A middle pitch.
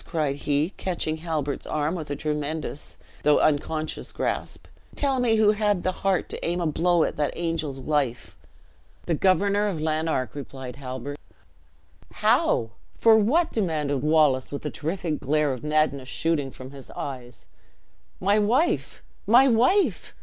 Yes: medium, 155 Hz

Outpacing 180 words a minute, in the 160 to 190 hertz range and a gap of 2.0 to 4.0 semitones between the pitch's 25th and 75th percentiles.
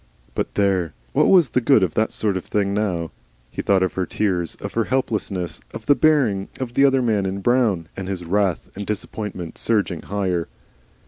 No: average, 195 wpm; low, 100 Hz; average, 3.6 semitones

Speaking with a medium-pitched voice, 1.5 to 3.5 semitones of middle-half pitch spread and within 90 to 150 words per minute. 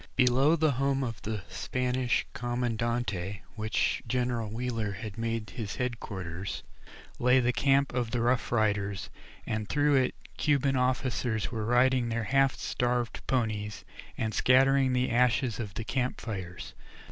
No: low, 120 Hz; average, 2.8 semitones; average, 145 wpm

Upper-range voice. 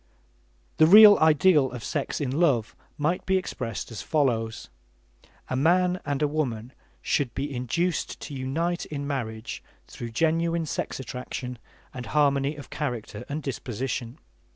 No: medium, 140 Hz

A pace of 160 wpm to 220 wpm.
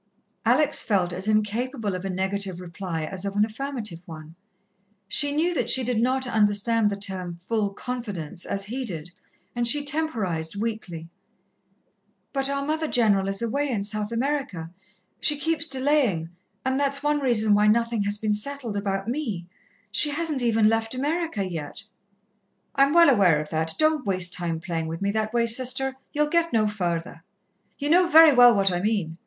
Yes: average, 175 wpm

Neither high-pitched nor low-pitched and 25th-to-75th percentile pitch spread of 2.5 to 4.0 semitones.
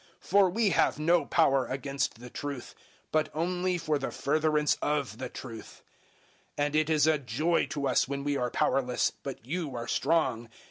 Yes: medium, 145 Hz; average, 3.1 semitones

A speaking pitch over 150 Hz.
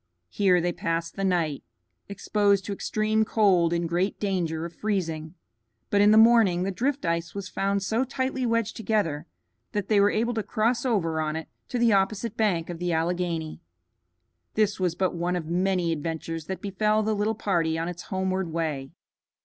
Yes: high, 190 Hz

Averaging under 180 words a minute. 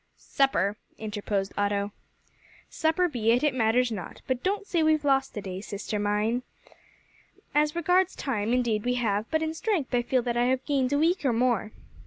No: average, 185 wpm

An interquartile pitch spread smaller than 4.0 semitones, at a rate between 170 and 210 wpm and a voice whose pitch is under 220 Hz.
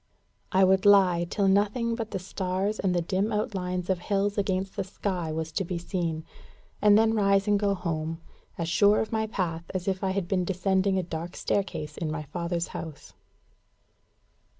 Yes: average, 2.8 semitones; average, 185 wpm; high, 190 Hz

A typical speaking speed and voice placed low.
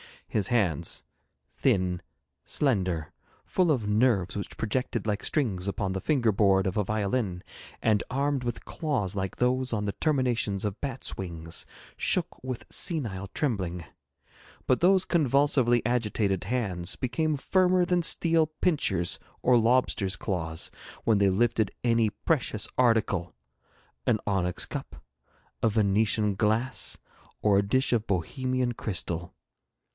No: slow, 130 wpm; low, 110 Hz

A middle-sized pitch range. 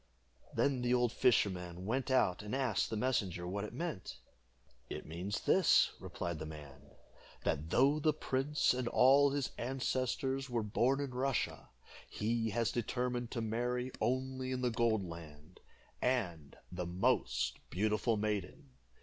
No: wide, 6.0 semitones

